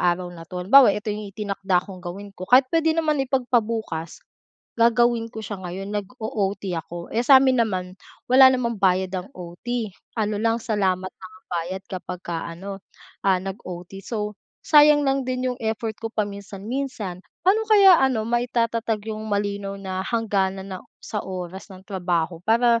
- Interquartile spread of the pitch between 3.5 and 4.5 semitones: Yes, average, 4.1 semitones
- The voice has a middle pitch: No, high, 210 Hz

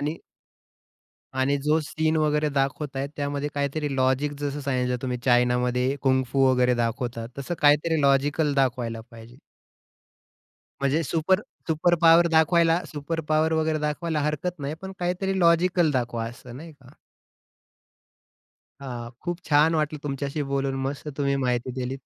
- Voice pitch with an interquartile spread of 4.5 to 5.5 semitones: No, average, 3.4 semitones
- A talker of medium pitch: Yes, medium, 145 Hz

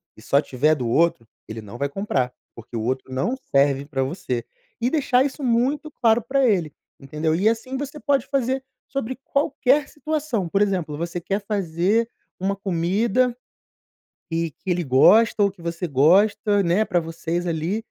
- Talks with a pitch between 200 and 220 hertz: No, high, 190 Hz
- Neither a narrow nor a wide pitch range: No, wide, 7.5 semitones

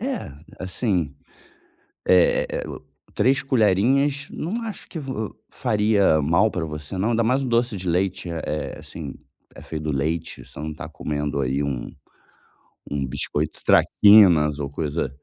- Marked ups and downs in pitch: Yes, wide, 7.6 semitones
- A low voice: Yes, very low, 95 Hz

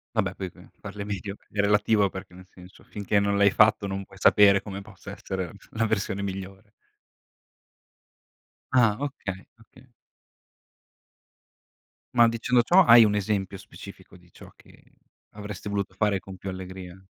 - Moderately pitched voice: No, low, 100 Hz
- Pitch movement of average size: No, narrow, 1.8 semitones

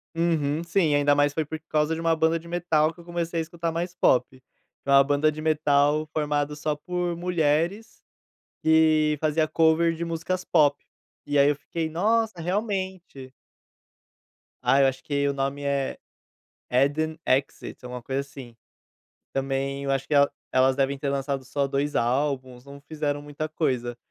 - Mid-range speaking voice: Yes, medium, 150 Hz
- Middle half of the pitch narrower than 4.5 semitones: Yes, average, 2.9 semitones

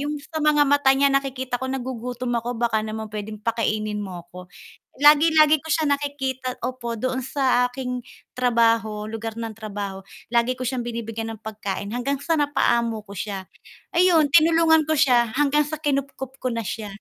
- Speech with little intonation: No, average, 4.3 semitones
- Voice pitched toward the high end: Yes, very high, 250 Hz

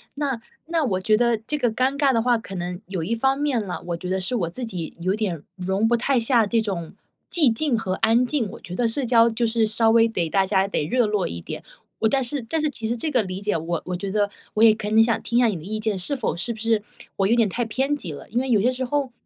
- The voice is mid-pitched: No, high, 225 Hz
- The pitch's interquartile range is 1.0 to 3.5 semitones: No, average, 4.3 semitones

